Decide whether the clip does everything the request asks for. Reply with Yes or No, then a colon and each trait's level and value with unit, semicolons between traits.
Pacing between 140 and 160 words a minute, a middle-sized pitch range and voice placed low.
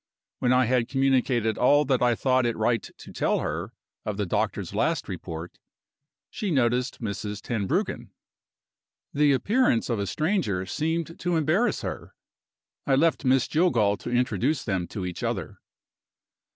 No: average, 150 wpm; wide, 5.7 semitones; low, 125 Hz